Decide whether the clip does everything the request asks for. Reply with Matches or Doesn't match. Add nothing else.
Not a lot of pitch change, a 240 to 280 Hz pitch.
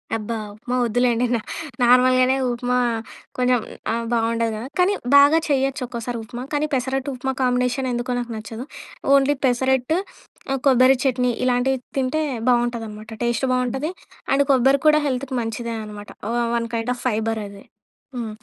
Matches